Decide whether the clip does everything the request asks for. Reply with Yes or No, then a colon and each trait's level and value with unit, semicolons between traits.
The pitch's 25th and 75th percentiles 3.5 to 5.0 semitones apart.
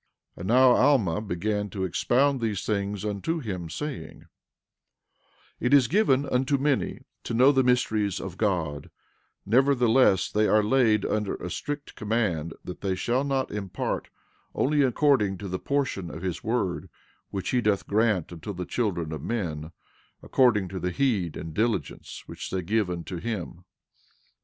No: wide, 5.6 semitones